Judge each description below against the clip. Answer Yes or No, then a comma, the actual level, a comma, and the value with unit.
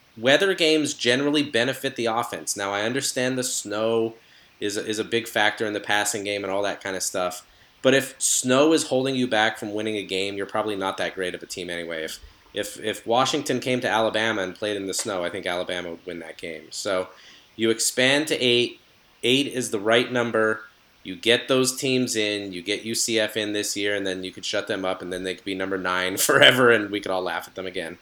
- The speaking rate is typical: No, fast, 235 wpm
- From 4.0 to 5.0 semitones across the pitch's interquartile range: Yes, average, 4.6 semitones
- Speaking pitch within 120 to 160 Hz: No, low, 110 Hz